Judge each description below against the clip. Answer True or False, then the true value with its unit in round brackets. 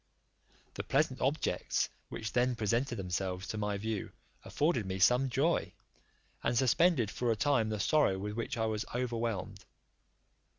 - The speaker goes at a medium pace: True (145 wpm)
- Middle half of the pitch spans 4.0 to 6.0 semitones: False (3.6 semitones)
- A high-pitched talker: False (115 Hz)